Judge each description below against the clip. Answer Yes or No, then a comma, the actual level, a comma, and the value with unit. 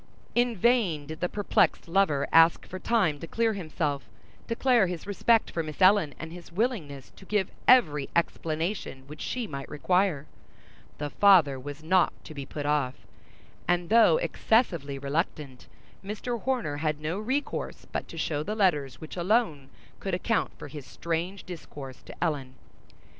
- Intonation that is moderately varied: No, wide, 5.8 semitones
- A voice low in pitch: No, medium, 170 Hz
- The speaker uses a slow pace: No, average, 160 wpm